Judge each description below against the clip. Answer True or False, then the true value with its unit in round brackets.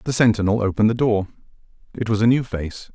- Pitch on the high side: False (110 Hz)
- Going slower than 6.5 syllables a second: False (6.6 syllables/s)